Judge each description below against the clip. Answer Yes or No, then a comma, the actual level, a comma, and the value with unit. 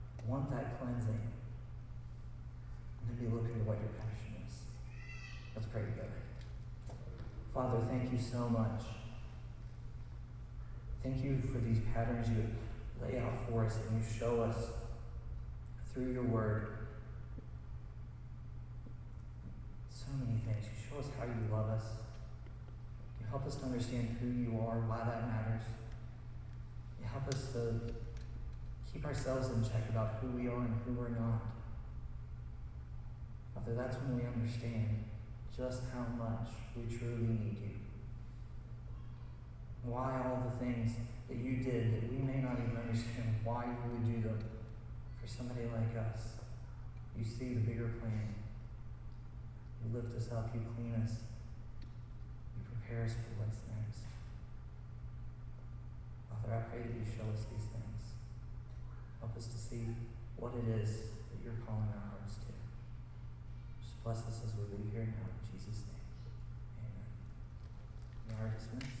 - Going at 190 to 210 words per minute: No, average, 145 wpm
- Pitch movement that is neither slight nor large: No, narrow, 1.2 semitones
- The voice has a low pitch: Yes, low, 115 Hz